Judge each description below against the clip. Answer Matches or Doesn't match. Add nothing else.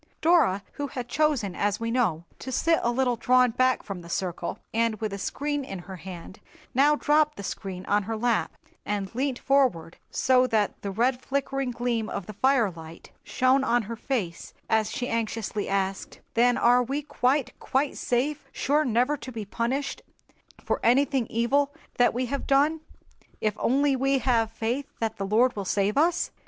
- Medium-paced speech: Matches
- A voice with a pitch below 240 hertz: Doesn't match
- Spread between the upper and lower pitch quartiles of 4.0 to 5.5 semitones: Matches